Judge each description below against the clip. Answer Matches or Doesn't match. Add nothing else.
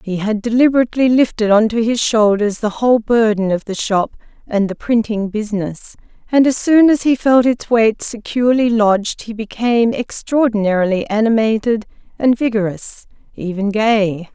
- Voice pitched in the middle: Doesn't match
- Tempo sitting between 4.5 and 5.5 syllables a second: Matches